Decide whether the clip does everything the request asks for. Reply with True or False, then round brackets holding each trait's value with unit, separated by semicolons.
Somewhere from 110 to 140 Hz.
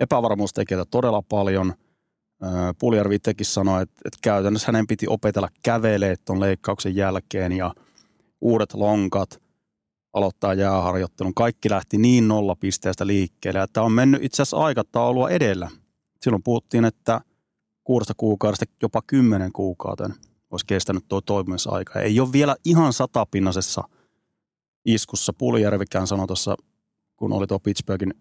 False (100 Hz)